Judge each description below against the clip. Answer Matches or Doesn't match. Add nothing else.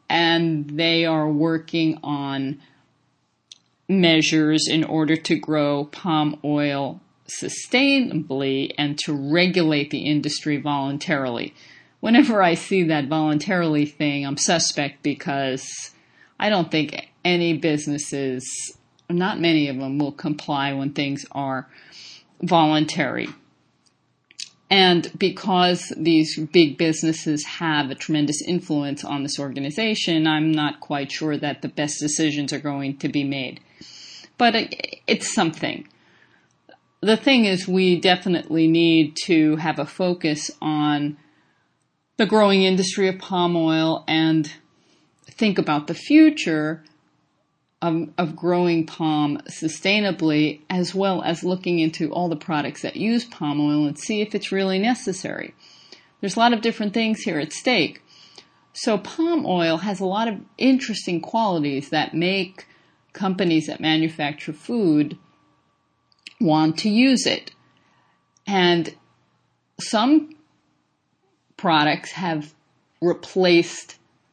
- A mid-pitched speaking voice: Matches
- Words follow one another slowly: Matches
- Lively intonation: Doesn't match